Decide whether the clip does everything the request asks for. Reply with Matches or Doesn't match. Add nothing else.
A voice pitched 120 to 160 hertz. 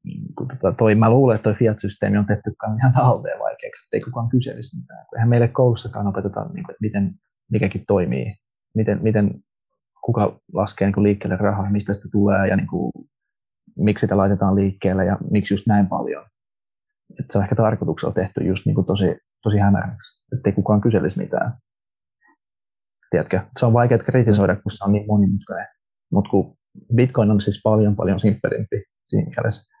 Doesn't match